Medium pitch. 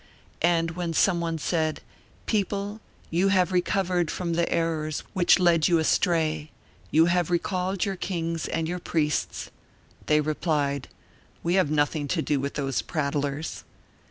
Yes: medium, 165 Hz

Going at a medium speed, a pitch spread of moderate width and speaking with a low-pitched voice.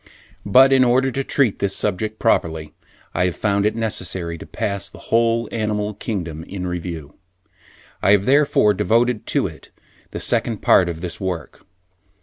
Yes: average, 160 wpm; average, 4.4 semitones; low, 100 Hz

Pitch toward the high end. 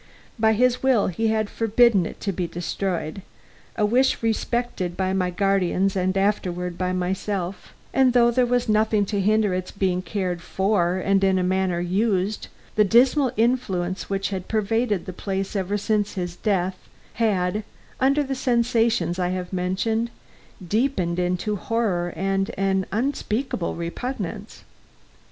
Yes: high, 195 Hz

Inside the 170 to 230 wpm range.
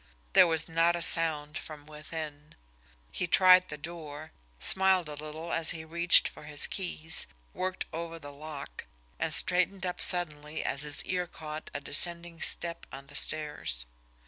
No: average, 160 wpm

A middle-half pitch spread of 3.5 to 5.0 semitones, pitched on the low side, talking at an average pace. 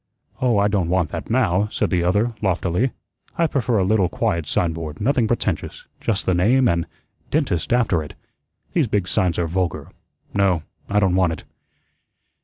Yes: average, 4.7 semitones; very low, 95 Hz; average, 170 wpm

